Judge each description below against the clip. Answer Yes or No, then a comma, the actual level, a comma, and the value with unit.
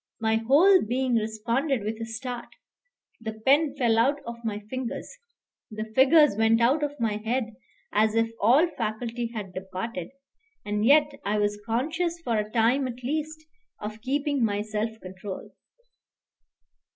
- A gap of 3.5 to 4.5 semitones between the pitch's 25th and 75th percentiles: Yes, average, 4.0 semitones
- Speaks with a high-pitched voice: Yes, high, 230 Hz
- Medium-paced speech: Yes, average, 150 wpm